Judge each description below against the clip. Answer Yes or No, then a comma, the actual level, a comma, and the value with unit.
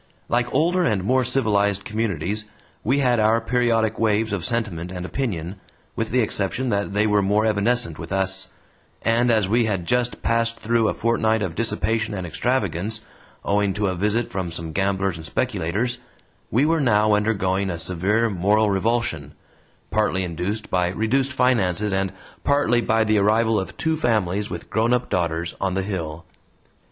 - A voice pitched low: Yes, low, 105 Hz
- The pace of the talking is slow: No, average, 165 wpm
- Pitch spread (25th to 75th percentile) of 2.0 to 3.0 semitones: No, average, 3.5 semitones